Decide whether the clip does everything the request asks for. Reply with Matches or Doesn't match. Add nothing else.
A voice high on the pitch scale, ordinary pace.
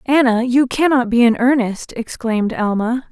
Matches